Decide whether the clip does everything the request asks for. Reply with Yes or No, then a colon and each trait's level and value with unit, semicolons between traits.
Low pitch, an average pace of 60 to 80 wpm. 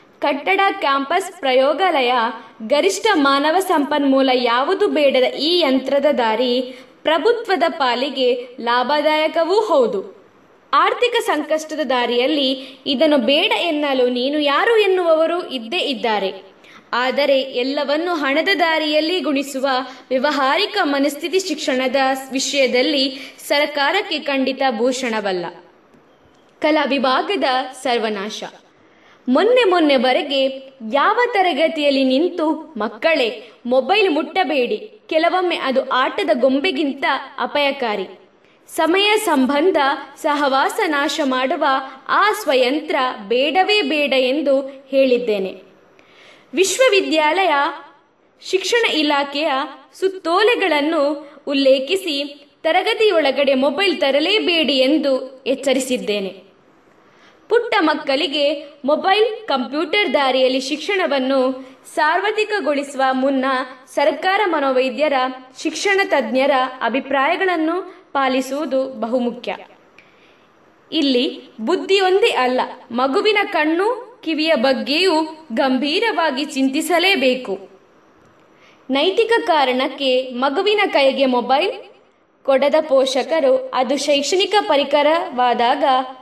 No: very high, 285 Hz; average, 75 wpm